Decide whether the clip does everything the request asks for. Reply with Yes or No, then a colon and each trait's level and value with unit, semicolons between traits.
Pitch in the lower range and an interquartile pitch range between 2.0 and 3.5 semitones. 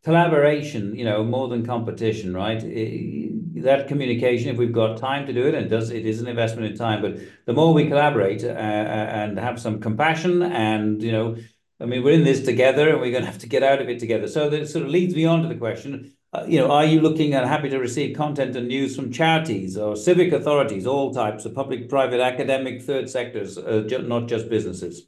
No: low, 125 Hz; average, 4.4 semitones